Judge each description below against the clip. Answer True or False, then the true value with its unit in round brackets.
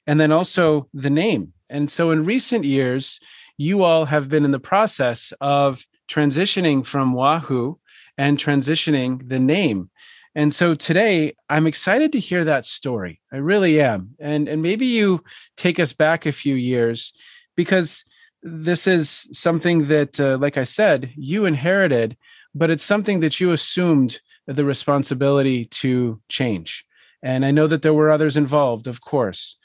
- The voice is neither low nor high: True (150 Hz)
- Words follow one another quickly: False (160 wpm)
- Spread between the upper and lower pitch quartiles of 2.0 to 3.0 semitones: False (4.1 semitones)